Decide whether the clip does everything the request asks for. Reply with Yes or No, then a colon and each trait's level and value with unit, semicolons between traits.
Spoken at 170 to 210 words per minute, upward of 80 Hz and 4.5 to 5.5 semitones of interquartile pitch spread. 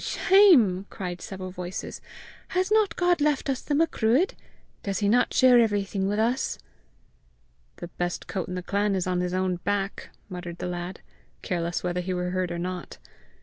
Yes: average, 175 wpm; high, 190 Hz; average, 5.2 semitones